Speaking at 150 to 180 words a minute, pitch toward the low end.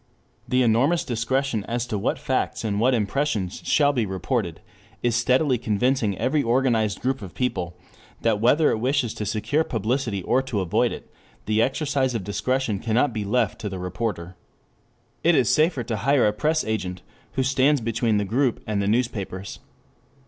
Yes: average, 170 wpm; low, 115 Hz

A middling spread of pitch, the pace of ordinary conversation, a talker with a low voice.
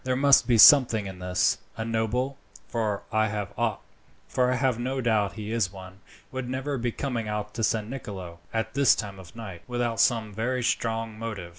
Yes: average, 3.1 semitones; average, 175 wpm; low, 115 Hz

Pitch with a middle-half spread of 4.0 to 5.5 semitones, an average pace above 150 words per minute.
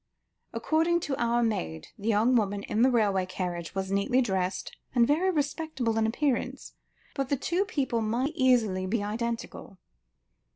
Yes: average, 5.2 semitones; average, 160 wpm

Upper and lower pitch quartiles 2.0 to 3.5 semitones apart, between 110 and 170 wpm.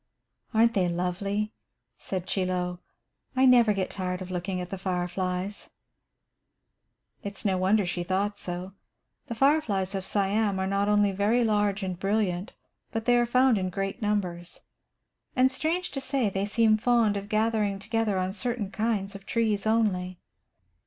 Yes: average, 3.1 semitones; average, 160 wpm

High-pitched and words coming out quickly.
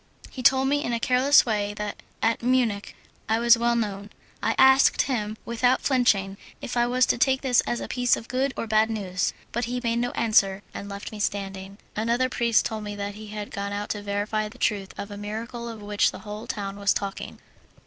Yes: high, 220 Hz; fast, 220 wpm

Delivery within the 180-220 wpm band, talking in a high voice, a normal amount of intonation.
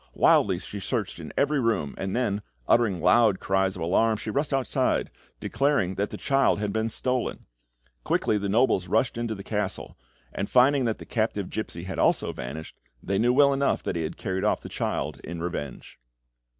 No: average, 190 wpm; low, 105 Hz; average, 4.6 semitones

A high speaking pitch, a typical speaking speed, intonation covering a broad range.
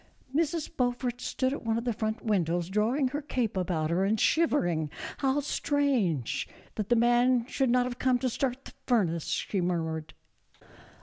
Yes: high, 240 Hz; average, 170 wpm; wide, 6.0 semitones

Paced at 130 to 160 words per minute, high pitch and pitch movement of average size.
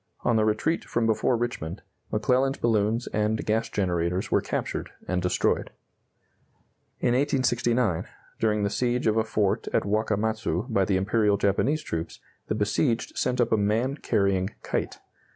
No: average, 150 wpm; low, 110 Hz; average, 3.0 semitones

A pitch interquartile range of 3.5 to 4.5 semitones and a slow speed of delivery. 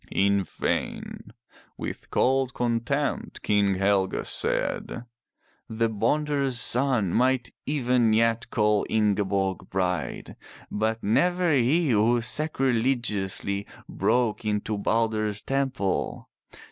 Yes: average, 4.0 semitones; slow, 95 wpm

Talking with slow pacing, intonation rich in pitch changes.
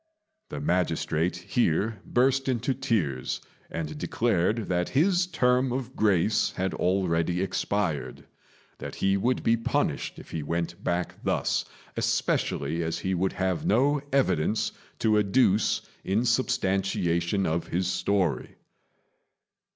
Yes: slow, 120 wpm; wide, 6.0 semitones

